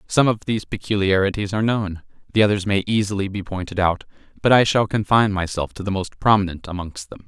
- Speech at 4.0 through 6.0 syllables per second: No, 6.2 syllables/s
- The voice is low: Yes, low, 100 Hz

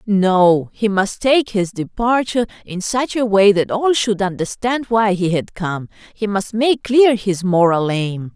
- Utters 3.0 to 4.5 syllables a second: Yes, 4.0 syllables/s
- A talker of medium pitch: No, high, 205 Hz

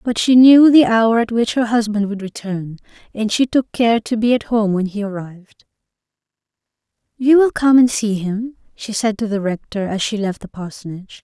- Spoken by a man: No, female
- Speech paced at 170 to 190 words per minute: No, fast, 205 wpm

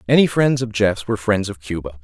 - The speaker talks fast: Yes, fast, 235 wpm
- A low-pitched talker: Yes, low, 105 Hz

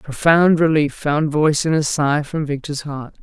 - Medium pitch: Yes, medium, 150 Hz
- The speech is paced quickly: No, average, 185 wpm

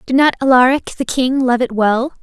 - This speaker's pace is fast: Yes, fast, 215 wpm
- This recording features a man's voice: No, female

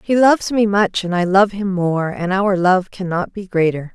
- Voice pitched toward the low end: No, high, 190 Hz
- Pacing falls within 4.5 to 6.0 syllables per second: Yes, 4.7 syllables/s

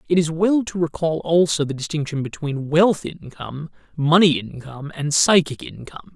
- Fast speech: No, average, 155 wpm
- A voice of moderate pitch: Yes, medium, 160 Hz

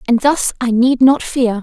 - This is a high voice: Yes, high, 245 Hz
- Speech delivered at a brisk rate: Yes, fast, 220 wpm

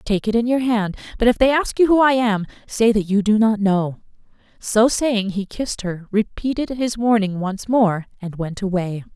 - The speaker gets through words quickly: Yes, fast, 210 wpm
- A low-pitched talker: No, high, 215 Hz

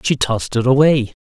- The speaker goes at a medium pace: Yes, average, 195 wpm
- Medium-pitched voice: No, low, 130 Hz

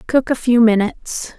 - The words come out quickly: No, average, 175 wpm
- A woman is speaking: Yes, female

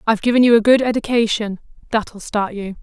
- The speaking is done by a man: No, female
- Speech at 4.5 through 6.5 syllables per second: Yes, 6.0 syllables/s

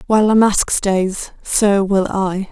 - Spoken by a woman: Yes, female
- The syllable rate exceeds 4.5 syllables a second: No, 3.6 syllables/s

